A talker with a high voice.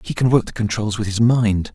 No: low, 110 Hz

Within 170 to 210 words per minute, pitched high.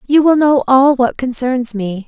Yes: average, 200 wpm; very high, 260 Hz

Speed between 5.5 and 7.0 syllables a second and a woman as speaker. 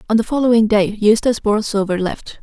Yes: 5.9 syllables/s; female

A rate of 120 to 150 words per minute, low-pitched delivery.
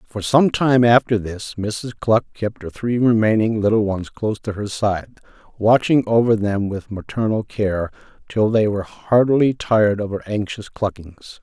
No: average, 170 wpm; low, 110 Hz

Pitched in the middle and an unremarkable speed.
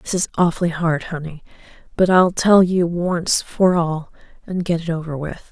Yes: medium, 170 Hz; average, 185 wpm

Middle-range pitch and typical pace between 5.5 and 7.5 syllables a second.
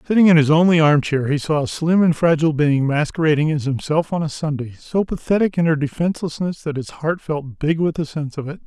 Yes: medium, 155 Hz; 6.0 syllables/s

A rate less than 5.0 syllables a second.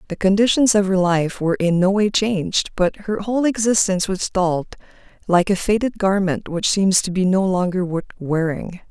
No: 5.2 syllables/s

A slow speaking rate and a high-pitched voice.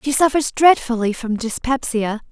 Yes: slow, 130 wpm; very high, 250 Hz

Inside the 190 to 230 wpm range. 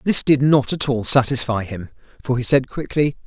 Yes: average, 200 wpm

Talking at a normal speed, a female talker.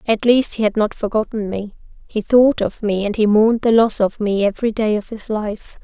No: fast, 235 wpm; female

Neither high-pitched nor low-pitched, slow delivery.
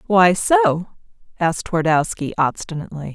Yes: medium, 180 Hz; slow, 95 wpm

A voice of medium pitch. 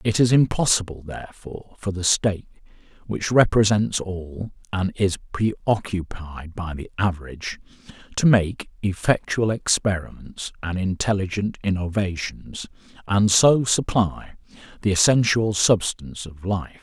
No: low, 100 Hz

